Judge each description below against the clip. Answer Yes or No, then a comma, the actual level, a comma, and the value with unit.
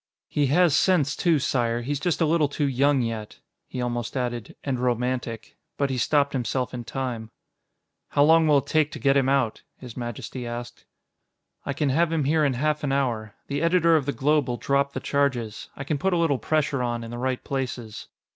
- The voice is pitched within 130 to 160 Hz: Yes, low, 135 Hz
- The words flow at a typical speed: No, fast, 210 wpm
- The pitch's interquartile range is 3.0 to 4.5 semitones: Yes, average, 3.5 semitones